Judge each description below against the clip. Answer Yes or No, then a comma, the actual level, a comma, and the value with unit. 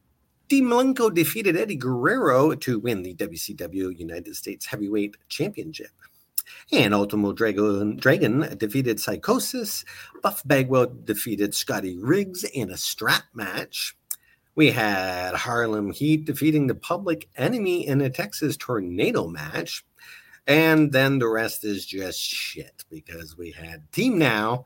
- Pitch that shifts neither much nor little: No, wide, 7.0 semitones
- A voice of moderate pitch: No, low, 120 Hz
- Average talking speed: No, slow, 125 wpm